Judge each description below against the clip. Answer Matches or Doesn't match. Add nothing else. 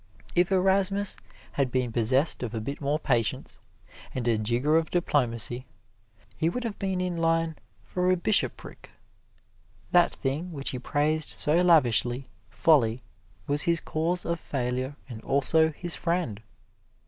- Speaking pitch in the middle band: Matches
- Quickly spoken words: Doesn't match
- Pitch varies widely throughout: Matches